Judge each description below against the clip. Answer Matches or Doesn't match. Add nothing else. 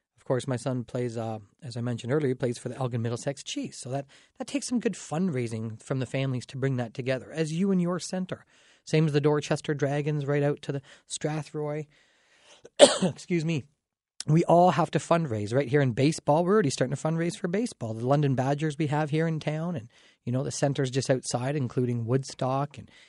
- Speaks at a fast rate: Matches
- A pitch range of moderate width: Matches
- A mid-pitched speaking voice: Matches